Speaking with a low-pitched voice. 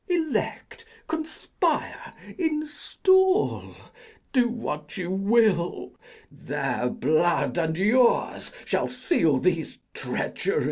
No: high, 205 Hz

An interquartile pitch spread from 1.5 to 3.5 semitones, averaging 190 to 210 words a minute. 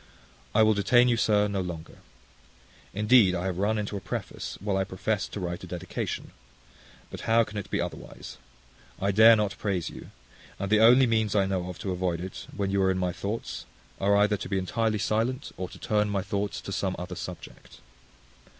Yes: narrow, 2.5 semitones; fast, 205 wpm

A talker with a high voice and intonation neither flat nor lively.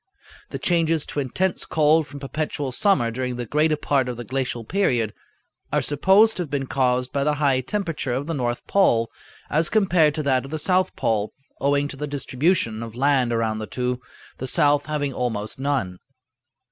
No: medium, 140 Hz; average, 3.6 semitones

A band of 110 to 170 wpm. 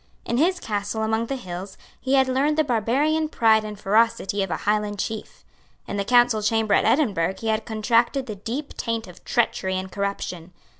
No: average, 190 wpm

